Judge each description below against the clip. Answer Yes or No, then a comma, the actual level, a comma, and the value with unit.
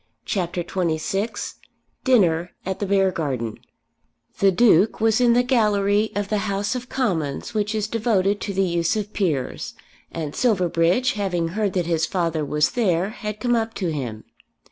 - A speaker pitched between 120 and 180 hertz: No, high, 195 Hz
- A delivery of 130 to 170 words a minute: Yes, average, 160 wpm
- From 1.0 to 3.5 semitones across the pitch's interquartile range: No, average, 4.3 semitones